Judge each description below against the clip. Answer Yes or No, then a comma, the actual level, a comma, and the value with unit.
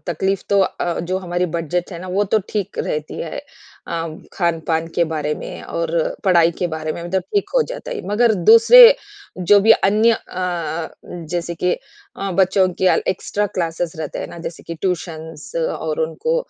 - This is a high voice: No, medium, 180 Hz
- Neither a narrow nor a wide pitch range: Yes, average, 3.2 semitones